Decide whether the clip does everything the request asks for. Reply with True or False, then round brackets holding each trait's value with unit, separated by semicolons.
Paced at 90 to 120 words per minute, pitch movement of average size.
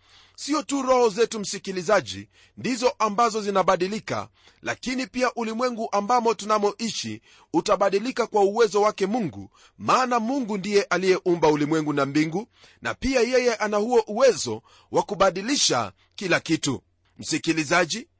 False (115 wpm; 5.9 semitones)